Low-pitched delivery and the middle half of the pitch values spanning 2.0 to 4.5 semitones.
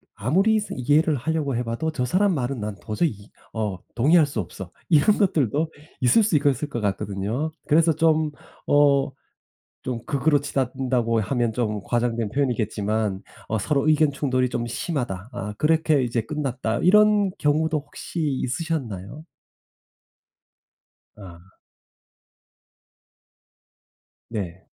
No: low, 130 Hz; wide, 5.6 semitones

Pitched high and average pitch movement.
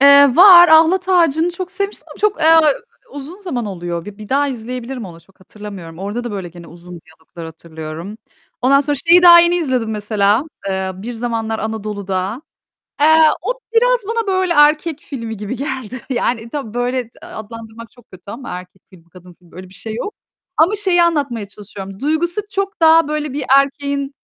No: high, 245 Hz; wide, 7.9 semitones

